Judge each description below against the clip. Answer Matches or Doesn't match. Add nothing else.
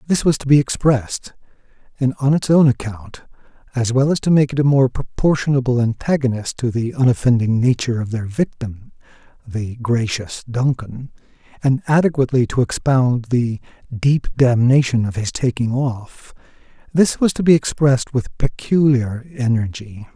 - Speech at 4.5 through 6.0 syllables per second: Matches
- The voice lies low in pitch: Matches